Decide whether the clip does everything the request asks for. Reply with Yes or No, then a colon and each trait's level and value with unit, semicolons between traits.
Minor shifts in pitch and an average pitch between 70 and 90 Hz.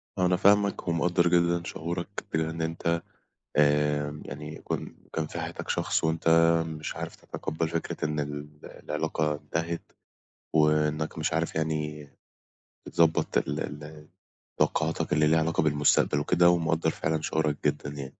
Yes: narrow, 1.7 semitones; very low, 80 Hz